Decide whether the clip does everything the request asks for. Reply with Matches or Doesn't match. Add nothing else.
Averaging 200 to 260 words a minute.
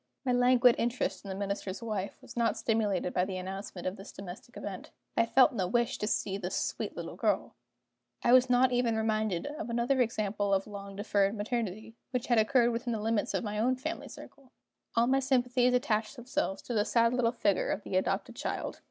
Matches